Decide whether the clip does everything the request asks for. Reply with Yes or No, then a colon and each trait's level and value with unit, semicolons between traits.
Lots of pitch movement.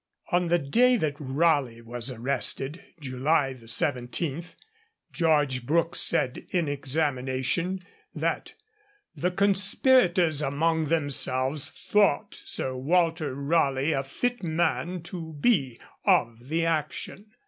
No: average, 4.5 semitones